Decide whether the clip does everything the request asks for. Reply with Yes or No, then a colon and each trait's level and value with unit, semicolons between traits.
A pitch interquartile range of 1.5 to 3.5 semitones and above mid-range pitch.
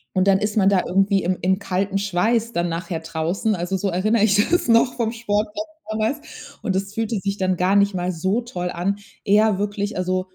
Yes: average, 2.9 semitones; high, 200 Hz